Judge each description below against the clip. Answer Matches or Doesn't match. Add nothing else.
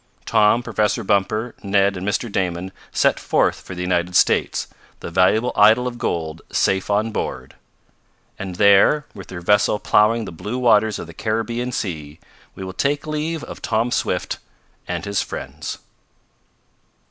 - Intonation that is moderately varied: Matches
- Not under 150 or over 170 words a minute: Matches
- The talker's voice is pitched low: Matches